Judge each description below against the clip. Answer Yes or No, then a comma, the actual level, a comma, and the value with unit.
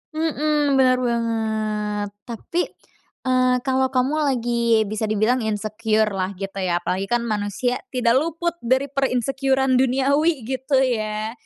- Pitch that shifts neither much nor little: Yes, average, 3.6 semitones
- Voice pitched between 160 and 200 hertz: No, high, 245 Hz